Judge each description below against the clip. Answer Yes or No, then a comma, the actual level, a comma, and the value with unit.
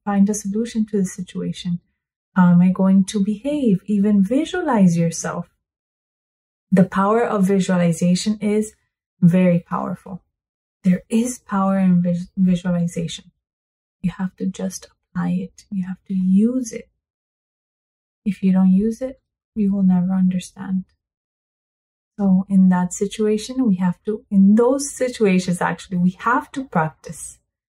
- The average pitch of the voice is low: No, high, 190 Hz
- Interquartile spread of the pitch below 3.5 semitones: Yes, average, 2.8 semitones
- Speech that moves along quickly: No, slow, 135 wpm